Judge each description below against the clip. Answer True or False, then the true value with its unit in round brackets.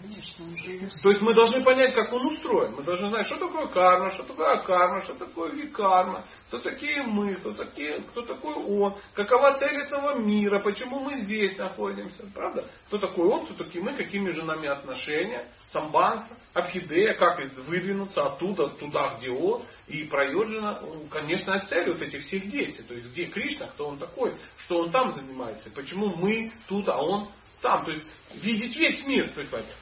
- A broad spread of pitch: True (6.2 semitones)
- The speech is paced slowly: False (175 wpm)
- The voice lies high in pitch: True (200 Hz)